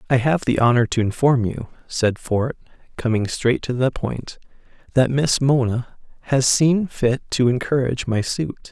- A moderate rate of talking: Yes, average, 165 wpm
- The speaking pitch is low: Yes, low, 130 Hz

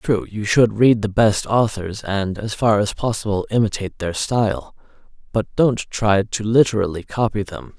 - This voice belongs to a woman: No, male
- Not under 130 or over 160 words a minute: No, average, 170 wpm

